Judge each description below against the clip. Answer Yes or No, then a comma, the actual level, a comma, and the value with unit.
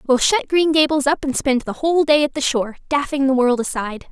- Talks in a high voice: Yes, very high, 280 Hz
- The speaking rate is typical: No, fast, 250 wpm